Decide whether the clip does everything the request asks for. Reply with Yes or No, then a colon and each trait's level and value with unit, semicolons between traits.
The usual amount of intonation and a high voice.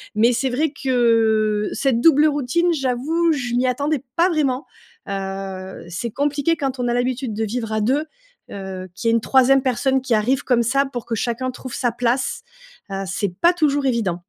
Yes: average, 3.7 semitones; very high, 250 Hz